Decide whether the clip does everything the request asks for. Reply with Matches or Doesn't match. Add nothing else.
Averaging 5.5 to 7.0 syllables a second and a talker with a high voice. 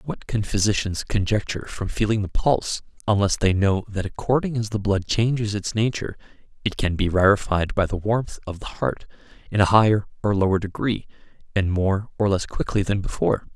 Doesn't match